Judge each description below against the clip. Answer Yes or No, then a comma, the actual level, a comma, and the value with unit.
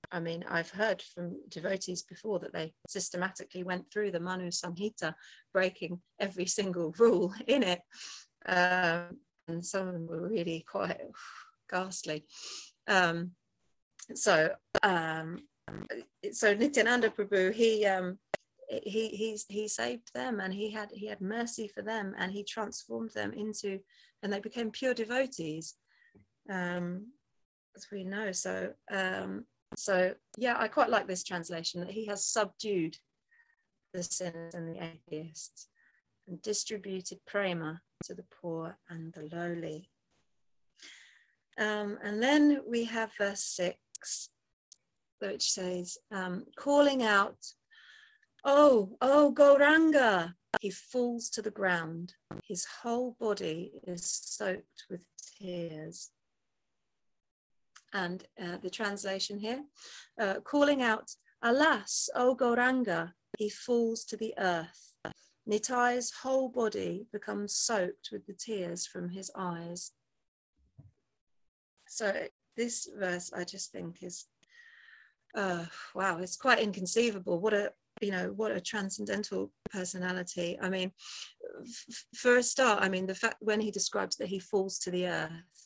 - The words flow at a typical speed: No, slow, 130 wpm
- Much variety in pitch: No, average, 4.0 semitones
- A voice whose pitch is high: Yes, high, 195 Hz